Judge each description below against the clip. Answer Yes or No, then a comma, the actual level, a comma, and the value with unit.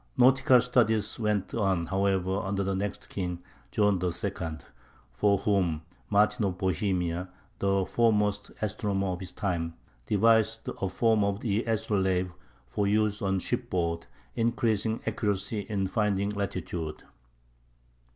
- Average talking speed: No, slow, 120 wpm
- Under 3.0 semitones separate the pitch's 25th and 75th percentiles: Yes, narrow, 2.4 semitones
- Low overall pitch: Yes, low, 100 Hz